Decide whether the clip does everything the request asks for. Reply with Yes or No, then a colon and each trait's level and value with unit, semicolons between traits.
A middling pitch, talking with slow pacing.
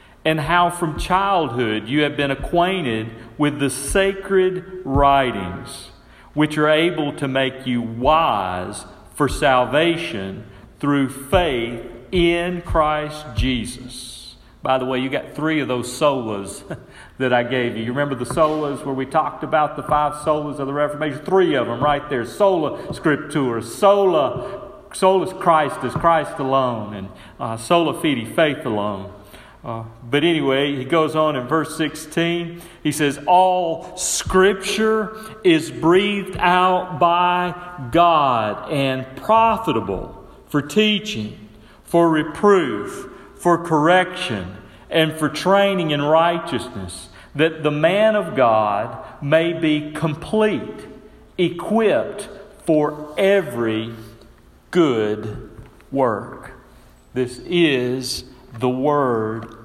Yes: medium, 150 Hz; slow, 120 wpm